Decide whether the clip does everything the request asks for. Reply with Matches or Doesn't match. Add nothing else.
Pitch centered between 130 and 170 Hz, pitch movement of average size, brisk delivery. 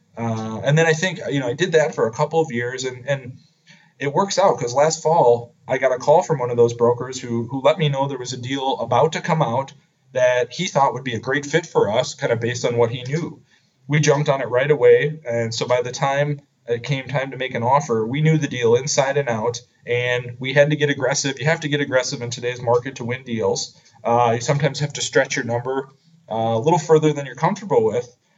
Matches